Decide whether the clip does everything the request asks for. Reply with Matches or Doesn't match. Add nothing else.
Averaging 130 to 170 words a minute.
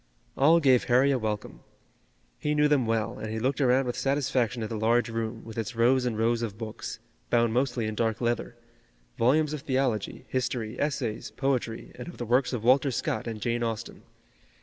Doesn't match